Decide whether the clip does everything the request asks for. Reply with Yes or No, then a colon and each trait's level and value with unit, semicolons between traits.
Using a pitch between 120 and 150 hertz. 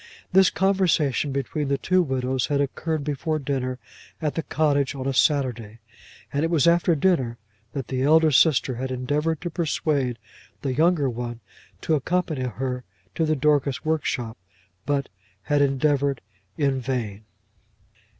Yes: medium, 140 Hz